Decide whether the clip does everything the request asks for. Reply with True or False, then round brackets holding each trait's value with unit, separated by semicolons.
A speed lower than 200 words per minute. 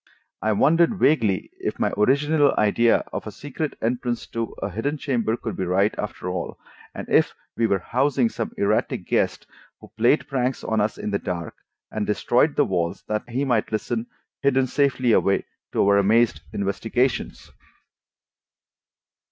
True (160 wpm)